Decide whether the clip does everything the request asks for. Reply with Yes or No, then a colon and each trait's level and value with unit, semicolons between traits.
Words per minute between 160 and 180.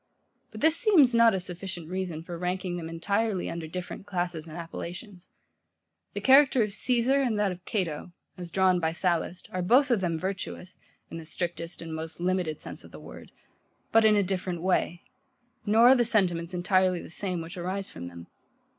No: average, 190 wpm